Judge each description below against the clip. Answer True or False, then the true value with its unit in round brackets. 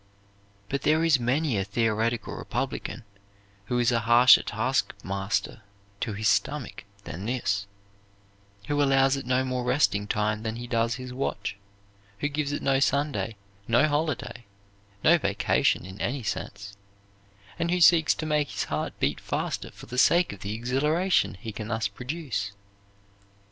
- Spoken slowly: False (155 wpm)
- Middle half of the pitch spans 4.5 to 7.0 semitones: True (5.0 semitones)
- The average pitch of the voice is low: True (125 Hz)